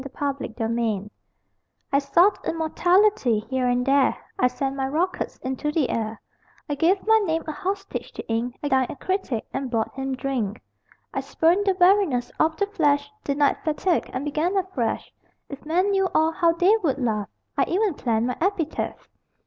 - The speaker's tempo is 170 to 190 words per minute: Yes, average, 175 wpm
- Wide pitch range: Yes, wide, 6.2 semitones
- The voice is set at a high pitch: Yes, very high, 290 Hz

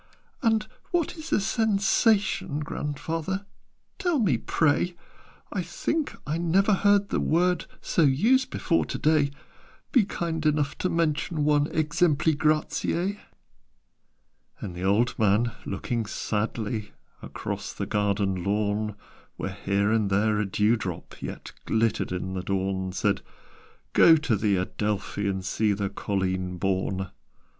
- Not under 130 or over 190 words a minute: Yes, slow, 135 wpm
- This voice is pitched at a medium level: No, low, 120 Hz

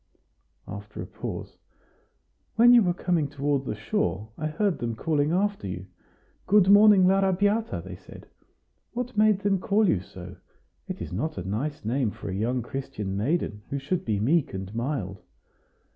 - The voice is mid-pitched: Yes, medium, 145 Hz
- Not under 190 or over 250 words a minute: No, average, 165 wpm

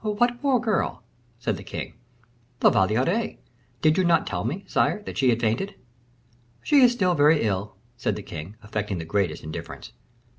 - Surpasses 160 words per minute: Yes, average, 175 wpm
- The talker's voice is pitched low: No, medium, 145 Hz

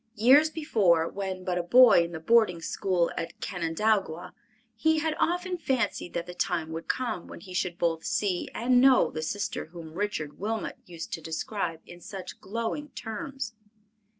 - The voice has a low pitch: No, high, 190 Hz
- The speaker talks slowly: No, average, 170 wpm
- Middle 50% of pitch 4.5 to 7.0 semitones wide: Yes, wide, 5.6 semitones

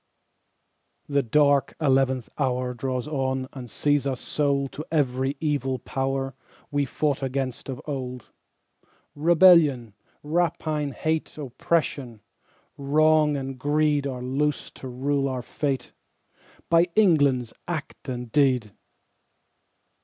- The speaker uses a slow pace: Yes, slow, 115 wpm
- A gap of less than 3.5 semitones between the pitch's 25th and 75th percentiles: Yes, narrow, 2.5 semitones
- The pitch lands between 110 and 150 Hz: Yes, medium, 140 Hz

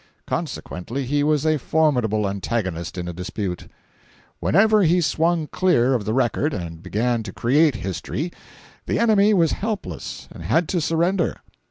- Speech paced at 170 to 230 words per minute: No, average, 150 wpm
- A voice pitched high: No, medium, 140 Hz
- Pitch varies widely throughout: Yes, wide, 8.1 semitones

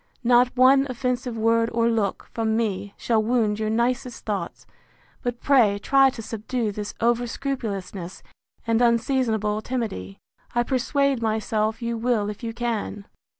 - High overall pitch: Yes, high, 230 Hz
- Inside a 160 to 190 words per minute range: No, average, 145 wpm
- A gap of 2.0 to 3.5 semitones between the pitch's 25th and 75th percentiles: Yes, narrow, 2.4 semitones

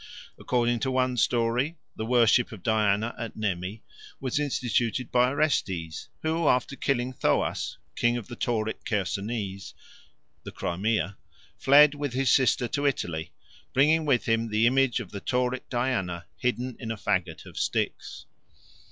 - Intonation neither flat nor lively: Yes, average, 3.4 semitones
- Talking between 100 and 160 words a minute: Yes, average, 145 wpm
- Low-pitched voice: Yes, low, 120 Hz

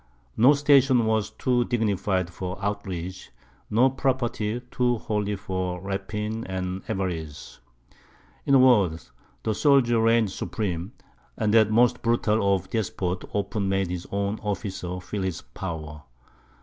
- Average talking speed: No, slow, 130 wpm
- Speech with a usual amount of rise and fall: Yes, average, 3.6 semitones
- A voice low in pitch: Yes, low, 100 Hz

